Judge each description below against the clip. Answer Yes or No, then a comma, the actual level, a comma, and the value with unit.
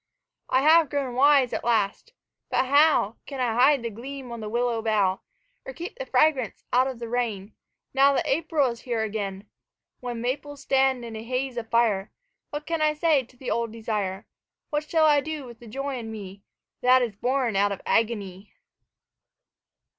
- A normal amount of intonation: Yes, average, 4.0 semitones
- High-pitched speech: Yes, high, 245 Hz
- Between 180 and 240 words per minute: Yes, average, 185 wpm